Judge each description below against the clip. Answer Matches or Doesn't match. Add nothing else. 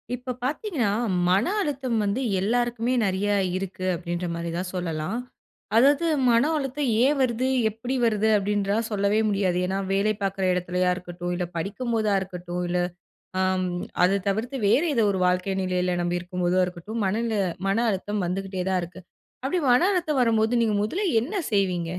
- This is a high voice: Matches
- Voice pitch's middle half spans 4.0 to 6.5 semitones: Matches